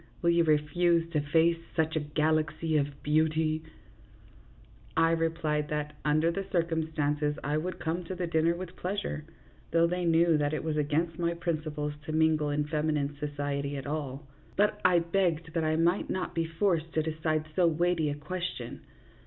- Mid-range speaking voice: Yes, medium, 160 Hz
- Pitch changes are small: Yes, narrow, 2.1 semitones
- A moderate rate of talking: Yes, average, 175 wpm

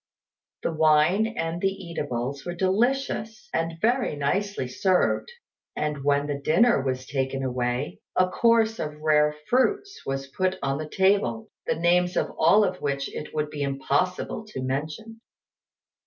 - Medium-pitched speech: Yes, medium, 160 Hz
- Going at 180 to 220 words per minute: No, average, 150 wpm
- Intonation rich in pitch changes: Yes, wide, 5.7 semitones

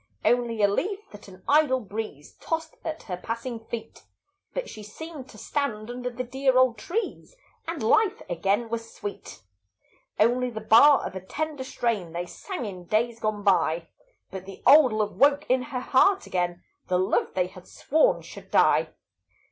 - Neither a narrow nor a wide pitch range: No, wide, 5.7 semitones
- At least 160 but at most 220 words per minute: Yes, average, 170 wpm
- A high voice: Yes, high, 235 Hz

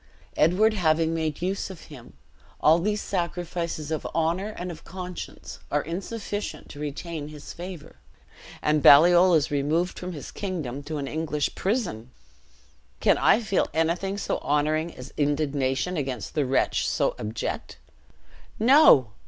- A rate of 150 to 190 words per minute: No, average, 140 wpm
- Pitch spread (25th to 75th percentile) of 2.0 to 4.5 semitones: Yes, average, 3.7 semitones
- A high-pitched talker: No, medium, 160 Hz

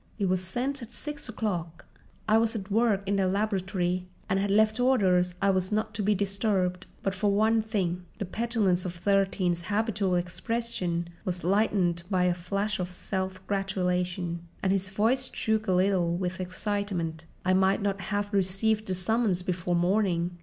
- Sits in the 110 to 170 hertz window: No, high, 195 Hz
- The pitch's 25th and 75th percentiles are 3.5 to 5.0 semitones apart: No, average, 2.8 semitones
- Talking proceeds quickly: No, average, 165 wpm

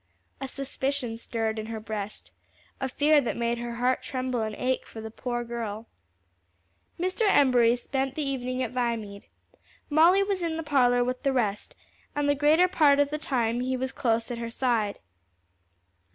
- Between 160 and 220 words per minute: Yes, average, 175 wpm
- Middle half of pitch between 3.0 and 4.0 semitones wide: Yes, average, 3.4 semitones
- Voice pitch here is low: No, very high, 250 Hz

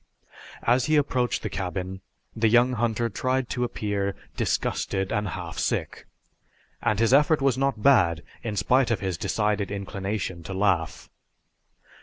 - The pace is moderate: Yes, average, 145 wpm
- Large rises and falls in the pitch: No, average, 4.4 semitones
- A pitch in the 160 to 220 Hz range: No, low, 105 Hz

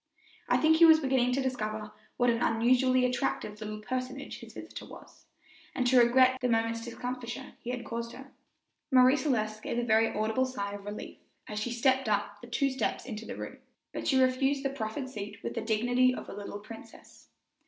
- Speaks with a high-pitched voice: Yes, high, 245 Hz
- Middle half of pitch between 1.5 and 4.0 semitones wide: Yes, average, 3.0 semitones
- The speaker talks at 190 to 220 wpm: Yes, average, 195 wpm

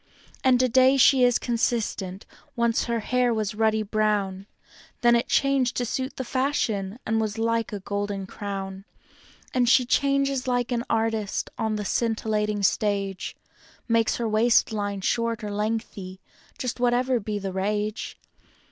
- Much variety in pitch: No, average, 3.0 semitones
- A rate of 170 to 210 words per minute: No, average, 145 wpm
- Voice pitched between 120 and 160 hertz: No, high, 225 Hz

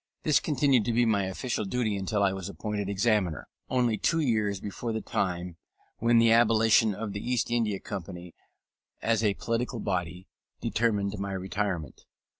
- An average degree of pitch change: Yes, average, 3.1 semitones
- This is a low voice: Yes, low, 105 Hz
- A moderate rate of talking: Yes, average, 160 wpm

